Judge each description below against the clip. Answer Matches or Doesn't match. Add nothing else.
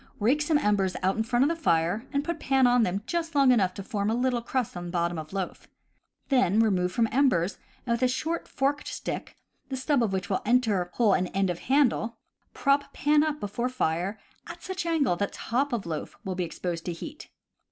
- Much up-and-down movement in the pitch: Matches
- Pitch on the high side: Matches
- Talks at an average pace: Doesn't match